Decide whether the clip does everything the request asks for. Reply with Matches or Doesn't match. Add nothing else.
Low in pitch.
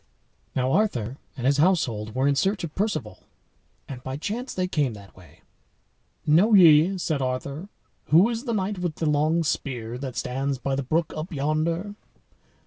Doesn't match